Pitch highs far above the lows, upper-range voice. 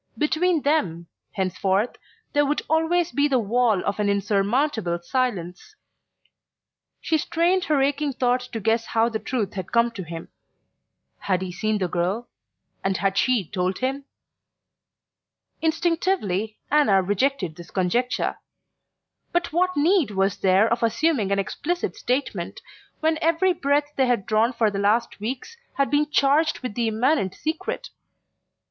Yes: wide, 6.9 semitones; high, 240 Hz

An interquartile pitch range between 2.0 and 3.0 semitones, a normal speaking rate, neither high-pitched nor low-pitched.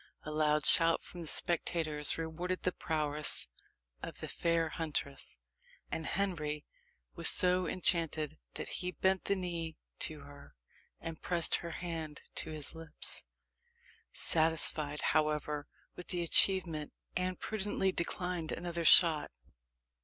No: average, 2.7 semitones; slow, 125 wpm; medium, 165 Hz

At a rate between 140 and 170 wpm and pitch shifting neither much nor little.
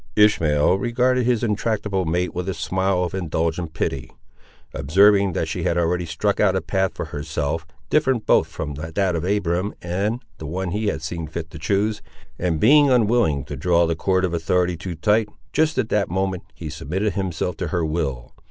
No: average, 185 wpm; average, 4.2 semitones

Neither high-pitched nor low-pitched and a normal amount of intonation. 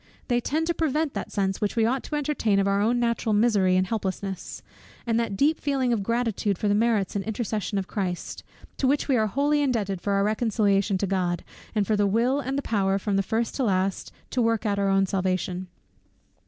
No: high, 210 Hz; average, 3.7 semitones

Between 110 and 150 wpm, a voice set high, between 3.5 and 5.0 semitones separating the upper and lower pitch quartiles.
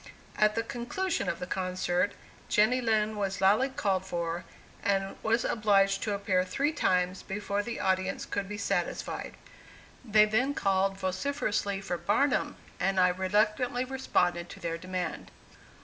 No: average, 145 wpm; high, 200 Hz; average, 2.7 semitones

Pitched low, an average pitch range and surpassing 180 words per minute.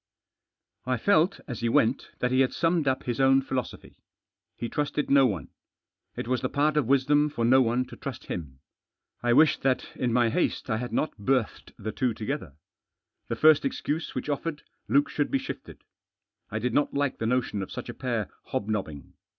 Yes: low, 130 Hz; average, 3.8 semitones; average, 190 wpm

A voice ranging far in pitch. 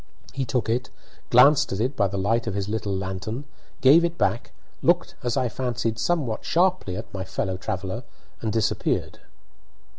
No: average, 4.8 semitones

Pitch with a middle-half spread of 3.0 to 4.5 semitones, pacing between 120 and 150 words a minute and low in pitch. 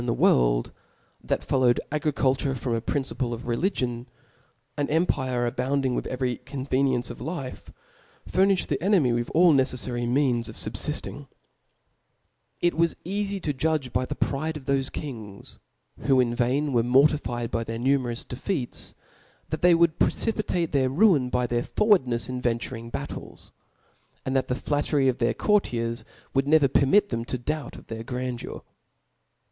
No: average, 3.9 semitones; average, 160 wpm; low, 130 Hz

